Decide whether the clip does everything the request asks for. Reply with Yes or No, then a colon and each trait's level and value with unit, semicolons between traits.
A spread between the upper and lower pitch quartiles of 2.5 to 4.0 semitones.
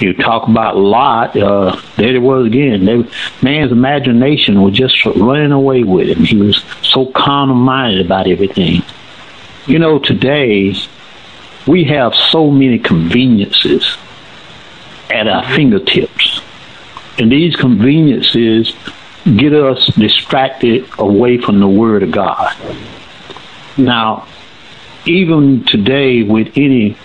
No: average, 4.5 semitones